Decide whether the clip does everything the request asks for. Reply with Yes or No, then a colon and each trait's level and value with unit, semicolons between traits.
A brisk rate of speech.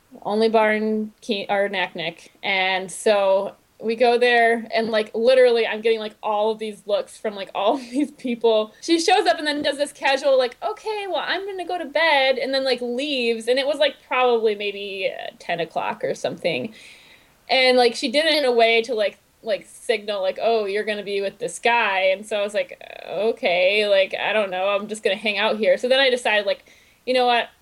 Yes: fast, 220 wpm